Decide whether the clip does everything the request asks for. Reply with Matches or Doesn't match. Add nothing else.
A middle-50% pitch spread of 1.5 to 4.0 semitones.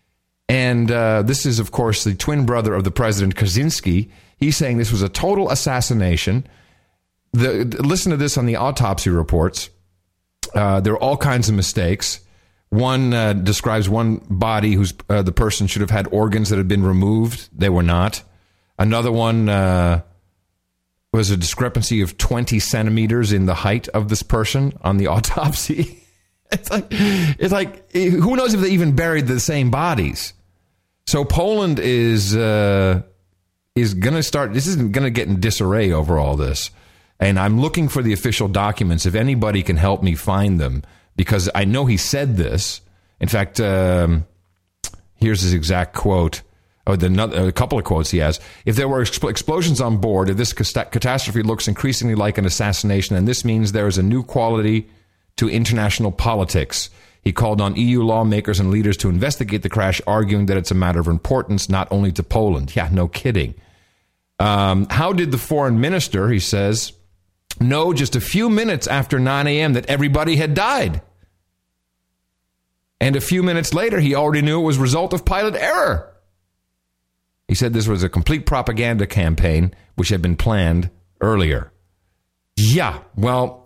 Doesn't match